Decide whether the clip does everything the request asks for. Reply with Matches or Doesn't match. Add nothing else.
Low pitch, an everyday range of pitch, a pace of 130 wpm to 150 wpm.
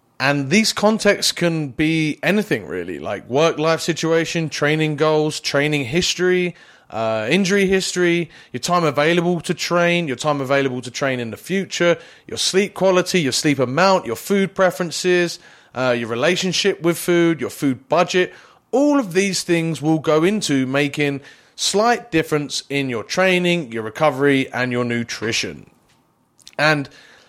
Doesn't match